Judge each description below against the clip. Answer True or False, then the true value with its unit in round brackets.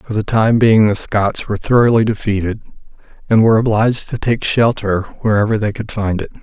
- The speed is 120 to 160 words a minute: False (185 wpm)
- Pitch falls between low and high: False (110 Hz)